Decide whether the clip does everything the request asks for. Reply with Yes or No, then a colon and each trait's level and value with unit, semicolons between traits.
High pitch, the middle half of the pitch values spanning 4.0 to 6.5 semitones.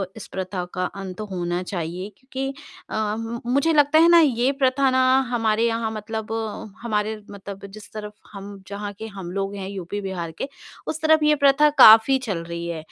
Yes: high, 215 Hz; average, 5.1 semitones